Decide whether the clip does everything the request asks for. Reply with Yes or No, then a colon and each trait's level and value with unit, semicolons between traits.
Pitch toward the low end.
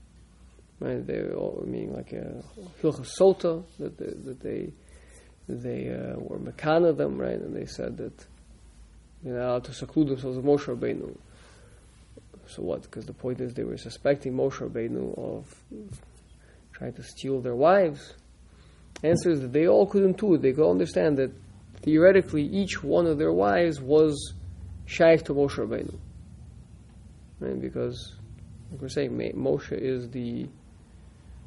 Yes: low, 130 Hz